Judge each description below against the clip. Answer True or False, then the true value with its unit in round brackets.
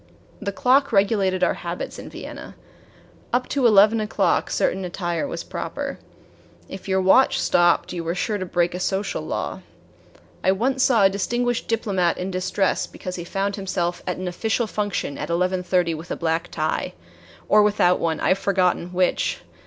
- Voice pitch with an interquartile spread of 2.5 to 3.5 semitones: True (2.8 semitones)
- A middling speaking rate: True (175 wpm)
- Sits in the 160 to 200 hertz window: True (190 Hz)